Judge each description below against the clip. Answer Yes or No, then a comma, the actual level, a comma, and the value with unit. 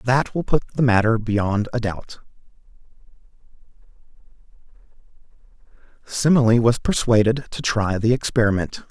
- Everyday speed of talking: No, slow, 100 wpm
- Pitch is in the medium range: No, low, 115 Hz